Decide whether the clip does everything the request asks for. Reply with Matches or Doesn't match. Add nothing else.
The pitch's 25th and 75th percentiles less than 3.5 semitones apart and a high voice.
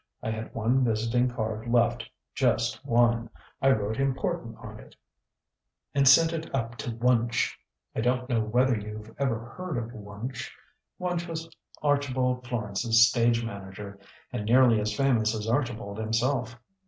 Doesn't match